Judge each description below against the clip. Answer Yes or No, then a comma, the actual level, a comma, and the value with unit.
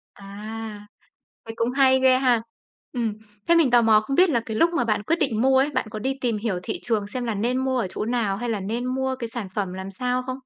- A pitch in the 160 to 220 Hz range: No, high, 235 Hz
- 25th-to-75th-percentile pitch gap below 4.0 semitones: Yes, average, 3.5 semitones